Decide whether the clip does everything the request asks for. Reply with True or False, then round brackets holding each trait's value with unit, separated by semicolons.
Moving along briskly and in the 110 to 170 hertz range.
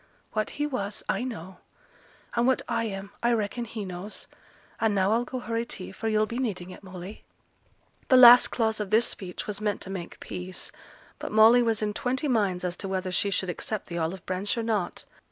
False (210 wpm; 210 Hz)